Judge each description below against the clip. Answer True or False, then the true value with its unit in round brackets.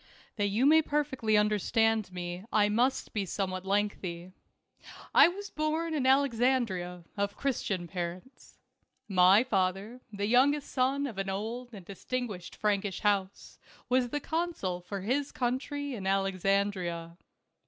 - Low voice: False (210 Hz)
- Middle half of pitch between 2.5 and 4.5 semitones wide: False (5.3 semitones)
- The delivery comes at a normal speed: False (130 wpm)